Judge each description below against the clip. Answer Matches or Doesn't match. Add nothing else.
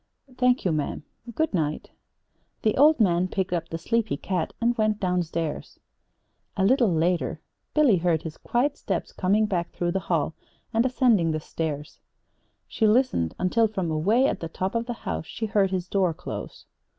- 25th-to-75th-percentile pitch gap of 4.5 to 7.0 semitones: Matches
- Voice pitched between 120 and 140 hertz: Doesn't match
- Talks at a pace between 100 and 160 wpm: Doesn't match